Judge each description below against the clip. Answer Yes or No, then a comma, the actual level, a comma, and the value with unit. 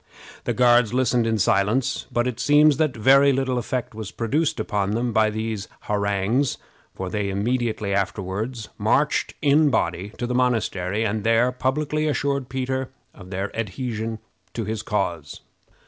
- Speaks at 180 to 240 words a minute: No, average, 155 wpm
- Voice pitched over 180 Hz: No, low, 115 Hz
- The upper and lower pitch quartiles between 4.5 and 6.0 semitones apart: No, average, 4.1 semitones